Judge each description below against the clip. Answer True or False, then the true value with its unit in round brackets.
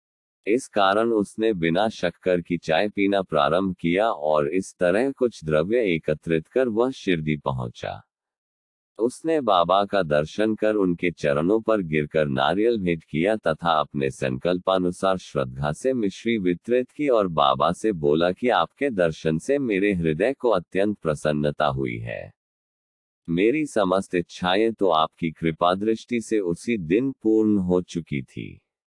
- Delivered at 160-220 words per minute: False (140 wpm)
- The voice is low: True (90 Hz)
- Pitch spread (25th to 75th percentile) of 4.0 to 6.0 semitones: True (5.6 semitones)